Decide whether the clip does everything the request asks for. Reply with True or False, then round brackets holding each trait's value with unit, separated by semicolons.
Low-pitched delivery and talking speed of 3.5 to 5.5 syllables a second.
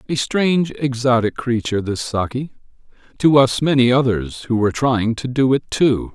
True (125 Hz; 5.0 syllables/s)